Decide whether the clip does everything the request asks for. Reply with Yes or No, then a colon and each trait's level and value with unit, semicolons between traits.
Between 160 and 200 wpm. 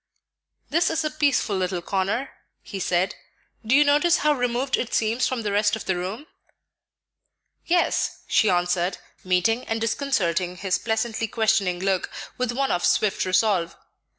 No: average, 150 wpm